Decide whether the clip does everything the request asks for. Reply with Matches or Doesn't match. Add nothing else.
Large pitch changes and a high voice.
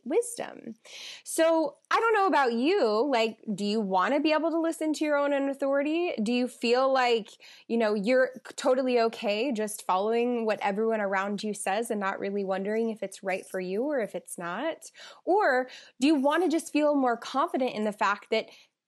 Matches